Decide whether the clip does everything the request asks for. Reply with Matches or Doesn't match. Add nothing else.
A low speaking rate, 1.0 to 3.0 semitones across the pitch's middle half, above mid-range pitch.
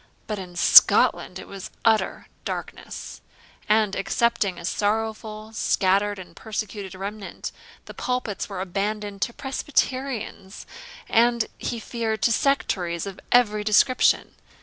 Matches